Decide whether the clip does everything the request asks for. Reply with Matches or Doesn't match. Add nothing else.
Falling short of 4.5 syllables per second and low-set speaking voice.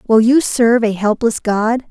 Doesn't match